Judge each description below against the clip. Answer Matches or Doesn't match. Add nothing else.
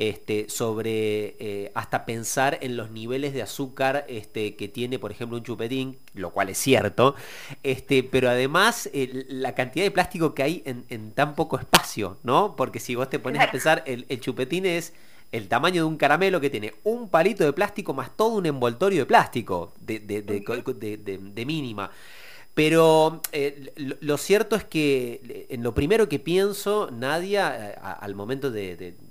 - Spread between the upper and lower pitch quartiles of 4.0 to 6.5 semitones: Matches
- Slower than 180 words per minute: Doesn't match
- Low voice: Matches